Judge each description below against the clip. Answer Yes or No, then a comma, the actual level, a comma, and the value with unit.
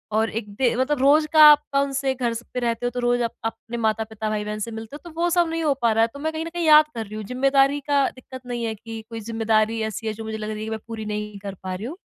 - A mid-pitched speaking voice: No, high, 230 Hz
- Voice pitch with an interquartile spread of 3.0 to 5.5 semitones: Yes, average, 4.1 semitones